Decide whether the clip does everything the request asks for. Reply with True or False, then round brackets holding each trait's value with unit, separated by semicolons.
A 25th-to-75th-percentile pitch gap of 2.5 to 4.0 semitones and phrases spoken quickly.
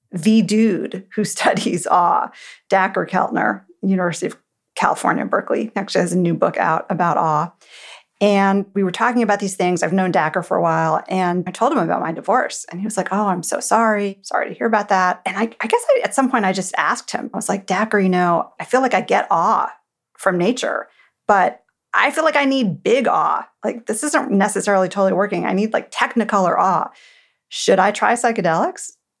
True (3.2 semitones; 210 wpm)